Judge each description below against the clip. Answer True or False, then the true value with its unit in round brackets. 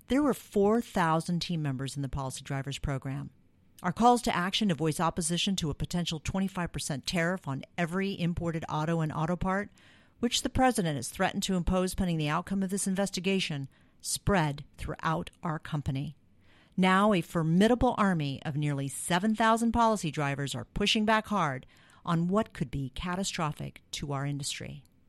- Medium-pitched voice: True (170 Hz)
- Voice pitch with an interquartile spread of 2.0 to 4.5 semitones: False (5.4 semitones)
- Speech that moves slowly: False (160 wpm)